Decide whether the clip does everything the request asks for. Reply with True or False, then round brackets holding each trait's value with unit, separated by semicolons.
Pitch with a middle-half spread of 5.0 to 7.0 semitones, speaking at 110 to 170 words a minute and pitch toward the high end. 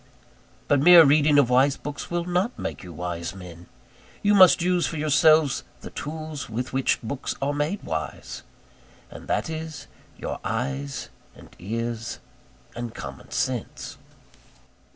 False (5.4 semitones; 140 wpm; 145 Hz)